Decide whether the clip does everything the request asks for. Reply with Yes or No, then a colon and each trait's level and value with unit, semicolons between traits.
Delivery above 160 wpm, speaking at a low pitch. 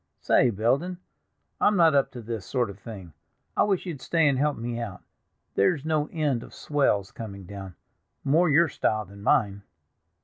Yes: average, 170 wpm; low, 120 Hz